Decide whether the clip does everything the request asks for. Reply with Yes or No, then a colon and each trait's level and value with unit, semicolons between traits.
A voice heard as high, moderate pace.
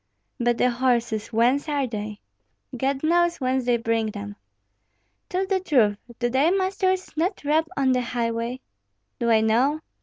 Yes: very high, 255 Hz; average, 155 wpm